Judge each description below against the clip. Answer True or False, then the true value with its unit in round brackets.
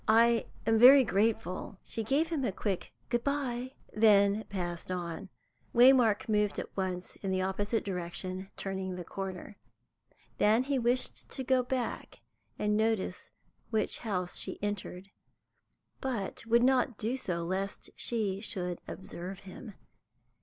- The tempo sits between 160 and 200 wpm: False (140 wpm)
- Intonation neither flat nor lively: True (4.1 semitones)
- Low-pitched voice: False (210 Hz)